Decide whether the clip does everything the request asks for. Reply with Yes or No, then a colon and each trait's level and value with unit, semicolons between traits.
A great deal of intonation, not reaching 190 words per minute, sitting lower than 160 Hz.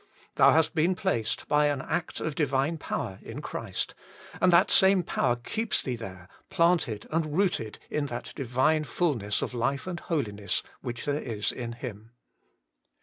Yes: wide, 5.9 semitones; average, 160 wpm; medium, 140 Hz